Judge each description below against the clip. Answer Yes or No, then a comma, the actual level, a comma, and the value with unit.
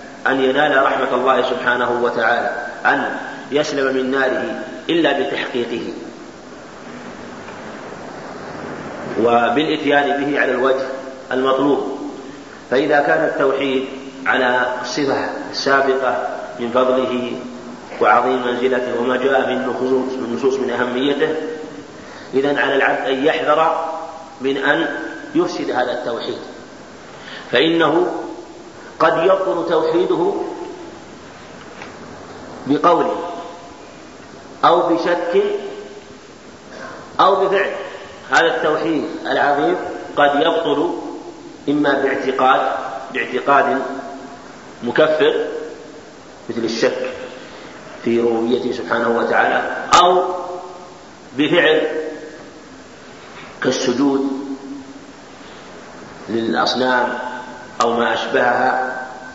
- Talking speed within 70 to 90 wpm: Yes, average, 75 wpm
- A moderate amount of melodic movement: Yes, average, 3.9 semitones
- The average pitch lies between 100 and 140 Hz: Yes, low, 135 Hz